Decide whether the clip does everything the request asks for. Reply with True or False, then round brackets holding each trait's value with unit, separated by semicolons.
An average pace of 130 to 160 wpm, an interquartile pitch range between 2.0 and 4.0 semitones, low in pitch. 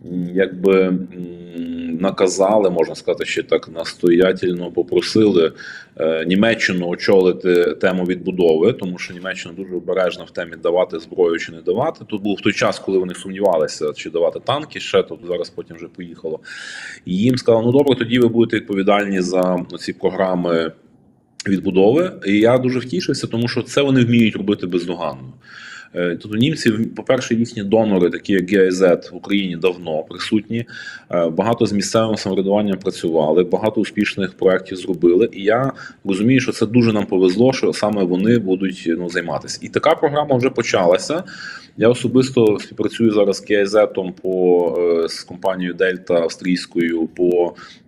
False (145 wpm; 4.5 semitones; 100 Hz)